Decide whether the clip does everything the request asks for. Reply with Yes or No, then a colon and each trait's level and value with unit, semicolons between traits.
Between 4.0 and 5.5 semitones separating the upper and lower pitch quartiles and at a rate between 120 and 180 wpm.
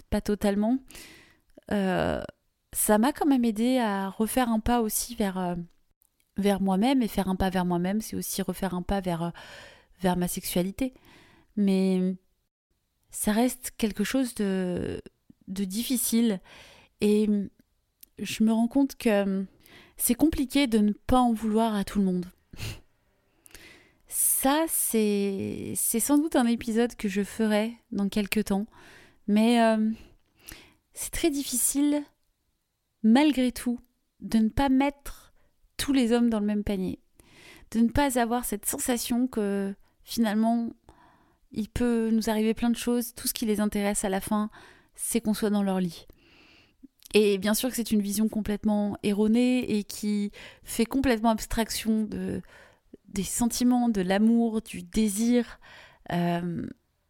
No: average, 3.3 semitones; slow, 145 wpm